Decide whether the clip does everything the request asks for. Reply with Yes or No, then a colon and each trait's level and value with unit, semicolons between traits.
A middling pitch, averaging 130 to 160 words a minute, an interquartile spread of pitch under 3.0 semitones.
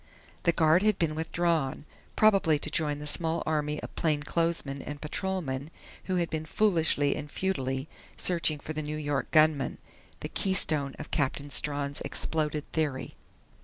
Yes: medium, 155 Hz; average, 150 wpm; narrow, 2.5 semitones